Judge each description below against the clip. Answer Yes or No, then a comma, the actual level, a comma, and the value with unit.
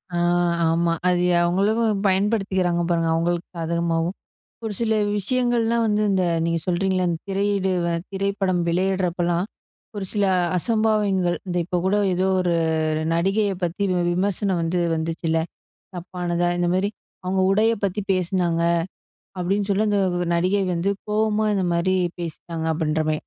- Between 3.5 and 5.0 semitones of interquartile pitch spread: No, average, 2.8 semitones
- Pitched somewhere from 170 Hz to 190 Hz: Yes, medium, 185 Hz